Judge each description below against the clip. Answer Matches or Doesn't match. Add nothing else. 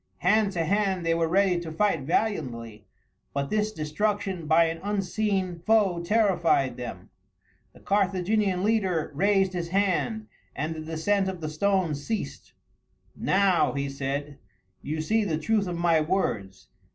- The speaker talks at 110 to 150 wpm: Matches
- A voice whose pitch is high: Doesn't match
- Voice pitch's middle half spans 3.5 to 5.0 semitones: Matches